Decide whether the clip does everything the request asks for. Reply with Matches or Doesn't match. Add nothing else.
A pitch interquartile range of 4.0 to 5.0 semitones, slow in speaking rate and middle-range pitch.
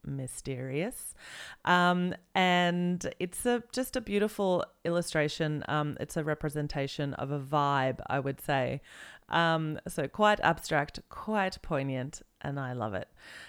Matches